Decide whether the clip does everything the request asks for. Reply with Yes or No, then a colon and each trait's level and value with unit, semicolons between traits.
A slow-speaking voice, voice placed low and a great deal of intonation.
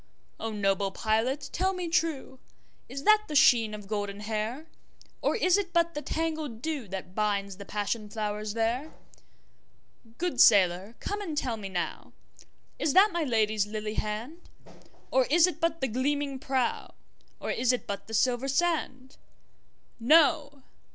No: slow, 130 wpm; very high, 255 Hz; wide, 6.7 semitones